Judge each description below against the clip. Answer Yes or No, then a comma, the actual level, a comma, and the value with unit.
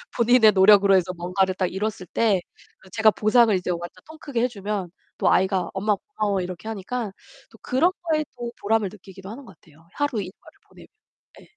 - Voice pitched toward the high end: Yes, high, 205 Hz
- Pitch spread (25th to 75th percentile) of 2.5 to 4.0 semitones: Yes, average, 3.6 semitones